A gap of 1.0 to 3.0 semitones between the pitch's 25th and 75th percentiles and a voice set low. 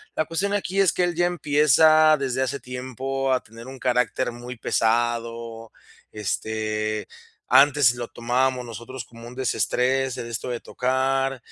Yes: narrow, 2.5 semitones; low, 125 Hz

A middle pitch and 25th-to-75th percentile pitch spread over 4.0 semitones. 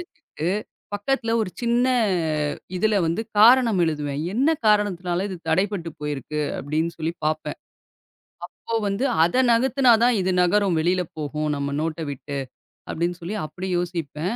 Yes: medium, 180 Hz; wide, 5.5 semitones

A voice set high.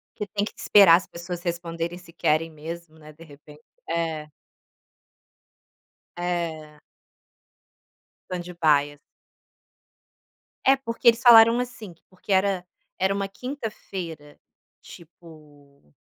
No: medium, 170 Hz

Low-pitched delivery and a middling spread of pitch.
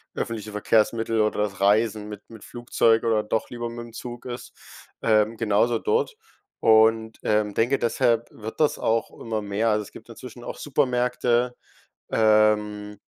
No: low, 110 Hz; narrow, 1.8 semitones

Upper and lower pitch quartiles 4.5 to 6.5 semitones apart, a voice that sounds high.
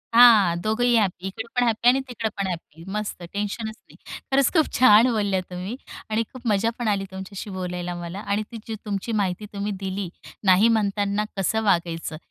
No: average, 2.9 semitones; high, 205 Hz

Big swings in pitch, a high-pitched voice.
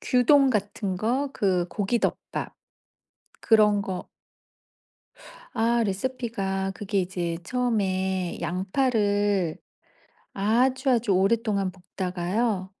No: average, 3.8 semitones; high, 205 Hz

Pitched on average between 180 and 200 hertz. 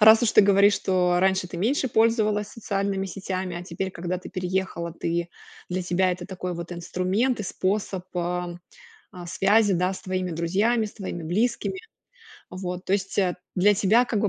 Yes: high, 190 Hz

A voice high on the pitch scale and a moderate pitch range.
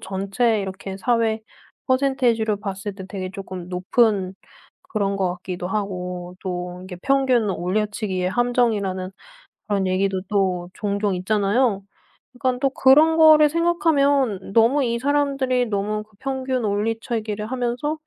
Yes: high, 210 Hz; average, 5.0 semitones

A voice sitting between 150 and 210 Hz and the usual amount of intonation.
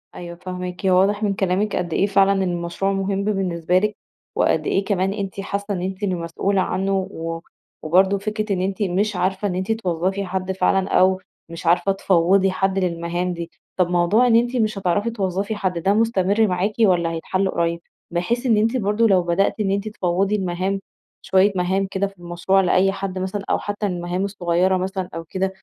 No: high, 190 Hz; narrow, 1.9 semitones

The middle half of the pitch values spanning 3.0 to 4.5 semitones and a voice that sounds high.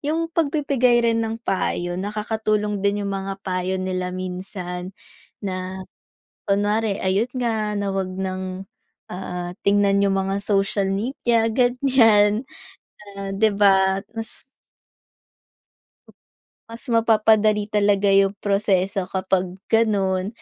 No: narrow, 2.6 semitones; high, 200 Hz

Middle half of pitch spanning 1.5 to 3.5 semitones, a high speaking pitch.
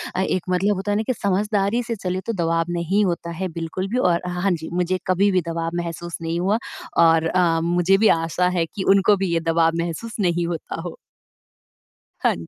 No: narrow, 2.6 semitones; medium, 180 Hz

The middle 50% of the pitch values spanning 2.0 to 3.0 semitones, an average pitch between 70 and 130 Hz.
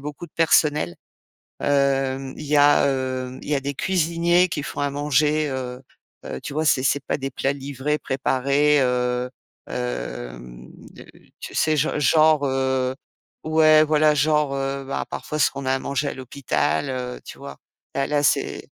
No: narrow, 2.4 semitones; medium, 140 Hz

